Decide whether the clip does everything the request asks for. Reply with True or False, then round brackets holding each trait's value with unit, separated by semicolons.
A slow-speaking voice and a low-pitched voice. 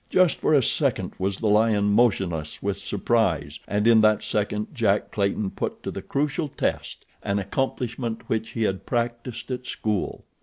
False (165 wpm; 110 Hz)